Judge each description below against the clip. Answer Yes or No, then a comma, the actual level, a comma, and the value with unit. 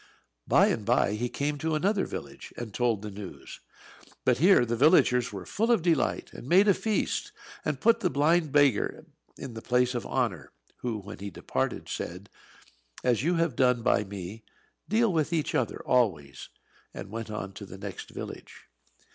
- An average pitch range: No, wide, 7.3 semitones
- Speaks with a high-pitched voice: No, low, 125 Hz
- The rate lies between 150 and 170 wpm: No, average, 180 wpm